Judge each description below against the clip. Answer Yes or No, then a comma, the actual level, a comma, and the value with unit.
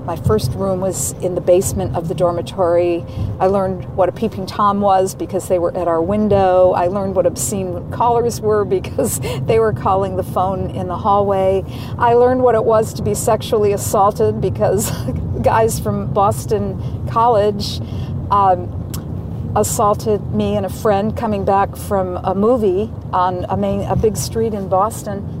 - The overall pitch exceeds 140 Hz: Yes, medium, 185 Hz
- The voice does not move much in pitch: No, average, 5.3 semitones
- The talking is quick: No, average, 170 wpm